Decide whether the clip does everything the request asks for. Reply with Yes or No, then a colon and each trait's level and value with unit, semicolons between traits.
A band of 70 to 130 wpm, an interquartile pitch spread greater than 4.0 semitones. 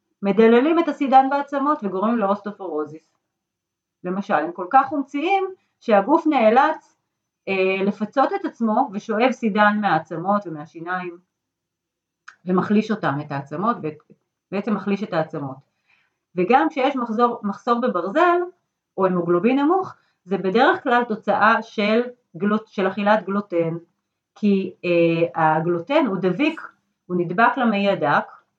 Yes: average, 115 wpm; wide, 5.6 semitones